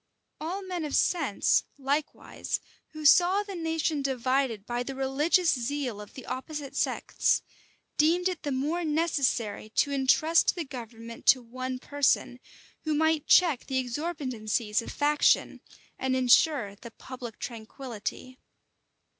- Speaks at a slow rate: Yes, slow, 130 wpm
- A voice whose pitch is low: No, very high, 275 Hz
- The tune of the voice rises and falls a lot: No, average, 4.1 semitones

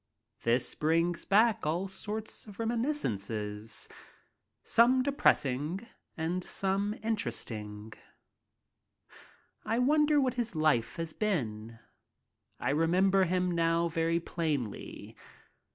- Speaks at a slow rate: Yes, slow, 100 wpm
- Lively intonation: Yes, wide, 7.7 semitones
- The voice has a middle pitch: Yes, medium, 170 Hz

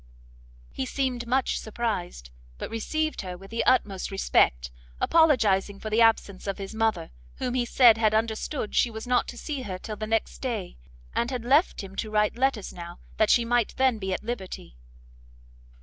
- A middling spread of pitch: Yes, average, 3.8 semitones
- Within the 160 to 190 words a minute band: Yes, average, 180 wpm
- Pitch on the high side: Yes, high, 225 Hz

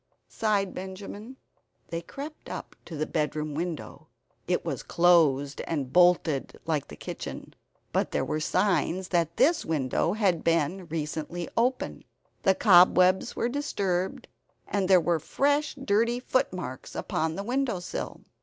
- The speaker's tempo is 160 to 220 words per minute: No, slow, 135 wpm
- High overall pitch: No, medium, 180 Hz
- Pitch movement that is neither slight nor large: Yes, average, 4.2 semitones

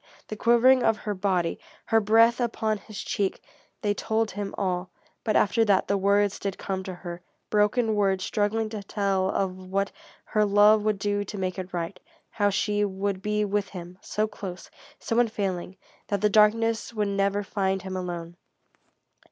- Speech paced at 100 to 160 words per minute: No, average, 175 wpm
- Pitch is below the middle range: No, high, 205 Hz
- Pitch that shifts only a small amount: Yes, narrow, 2.0 semitones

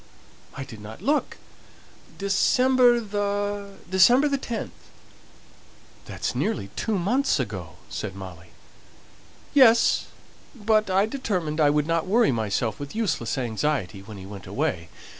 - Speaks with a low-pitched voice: No, medium, 185 Hz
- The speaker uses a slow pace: Yes, slow, 120 wpm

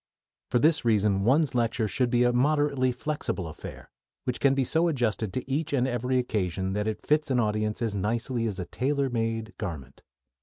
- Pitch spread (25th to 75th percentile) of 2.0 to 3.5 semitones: No, average, 4.0 semitones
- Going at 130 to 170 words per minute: No, average, 190 wpm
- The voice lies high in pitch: No, low, 120 Hz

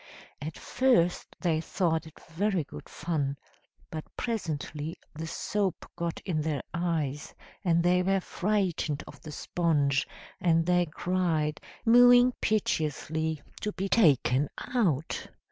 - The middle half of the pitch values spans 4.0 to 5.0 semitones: No, average, 3.4 semitones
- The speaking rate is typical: No, slow, 125 wpm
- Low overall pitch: No, medium, 165 Hz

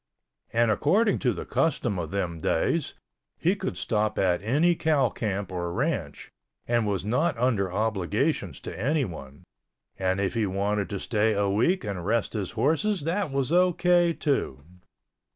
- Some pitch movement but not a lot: No, wide, 7.5 semitones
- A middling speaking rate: Yes, average, 155 wpm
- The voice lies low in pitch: Yes, low, 110 Hz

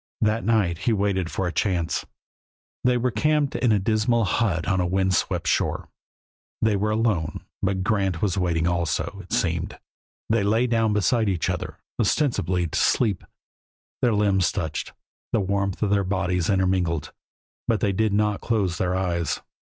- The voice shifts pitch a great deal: No, average, 3.3 semitones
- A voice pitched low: Yes, low, 100 Hz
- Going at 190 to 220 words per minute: No, average, 165 wpm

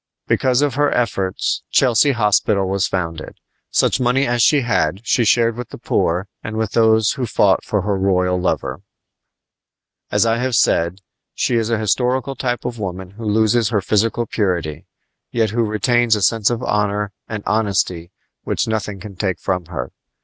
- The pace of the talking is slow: No, average, 180 wpm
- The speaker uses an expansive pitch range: No, average, 3.7 semitones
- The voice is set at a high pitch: No, low, 105 Hz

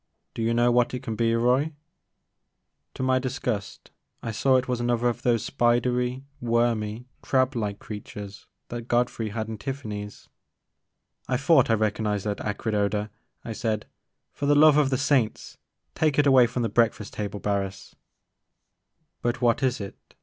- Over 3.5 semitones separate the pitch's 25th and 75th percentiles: No, average, 3.2 semitones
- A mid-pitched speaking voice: No, low, 120 Hz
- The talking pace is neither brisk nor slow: Yes, average, 165 wpm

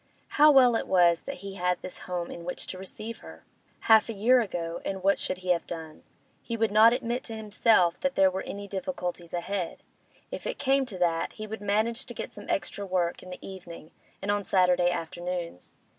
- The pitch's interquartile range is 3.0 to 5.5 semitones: Yes, average, 3.9 semitones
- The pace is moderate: No, fast, 210 wpm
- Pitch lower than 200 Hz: Yes, high, 190 Hz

